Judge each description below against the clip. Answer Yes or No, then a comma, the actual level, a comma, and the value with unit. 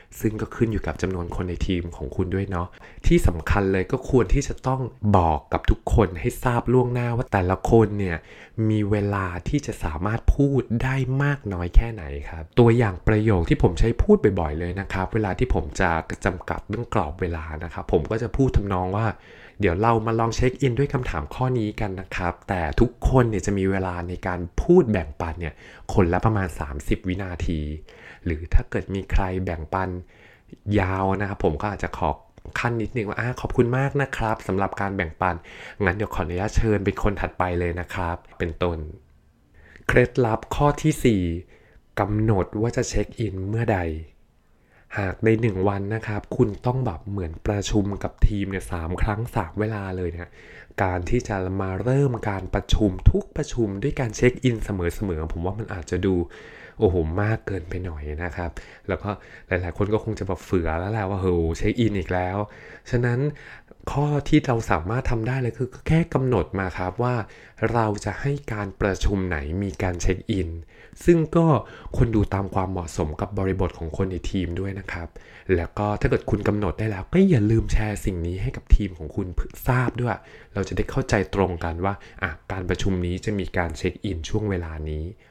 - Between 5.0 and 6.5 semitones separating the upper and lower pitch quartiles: No, average, 4.2 semitones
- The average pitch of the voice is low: Yes, low, 100 Hz